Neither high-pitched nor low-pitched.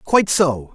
Yes: medium, 155 Hz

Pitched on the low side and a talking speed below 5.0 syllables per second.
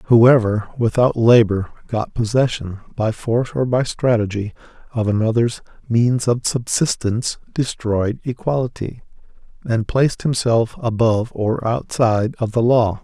Yes: low, 115 Hz; 4.5 syllables/s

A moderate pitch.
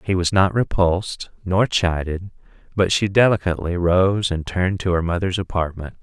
No: very low, 90 Hz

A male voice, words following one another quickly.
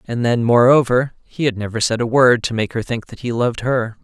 Yes: male; fast, 255 wpm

